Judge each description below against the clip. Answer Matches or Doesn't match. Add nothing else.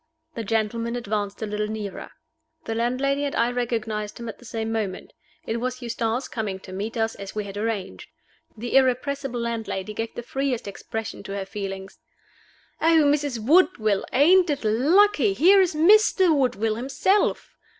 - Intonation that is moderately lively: Matches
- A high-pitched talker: Matches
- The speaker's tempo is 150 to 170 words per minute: Matches